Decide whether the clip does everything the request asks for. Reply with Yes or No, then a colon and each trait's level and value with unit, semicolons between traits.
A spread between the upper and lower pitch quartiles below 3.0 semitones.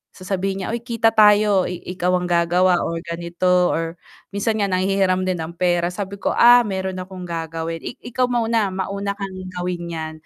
Yes: narrow, 2.5 semitones